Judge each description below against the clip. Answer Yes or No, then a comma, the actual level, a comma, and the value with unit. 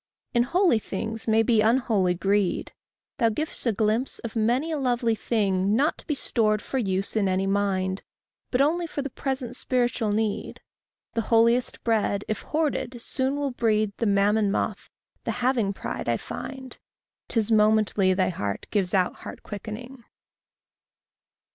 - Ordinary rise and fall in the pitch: Yes, average, 3.7 semitones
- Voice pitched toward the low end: No, high, 225 Hz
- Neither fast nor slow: Yes, average, 155 wpm